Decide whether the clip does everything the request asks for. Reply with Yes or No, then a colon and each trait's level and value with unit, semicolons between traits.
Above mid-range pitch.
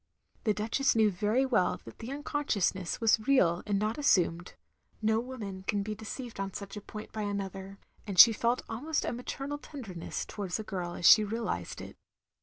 Yes: high, 215 Hz